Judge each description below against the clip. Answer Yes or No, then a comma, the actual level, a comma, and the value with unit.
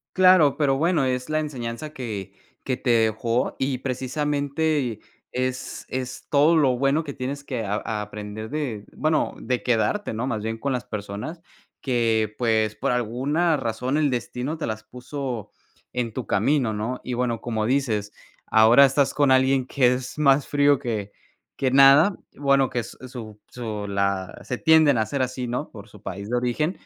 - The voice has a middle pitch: No, low, 125 Hz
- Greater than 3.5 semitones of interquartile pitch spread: Yes, average, 4.0 semitones